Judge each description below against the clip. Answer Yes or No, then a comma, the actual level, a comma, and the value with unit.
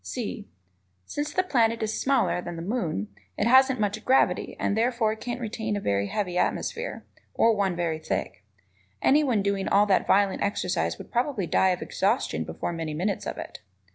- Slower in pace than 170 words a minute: No, average, 175 wpm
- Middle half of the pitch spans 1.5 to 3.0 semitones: No, average, 5.2 semitones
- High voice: Yes, high, 205 Hz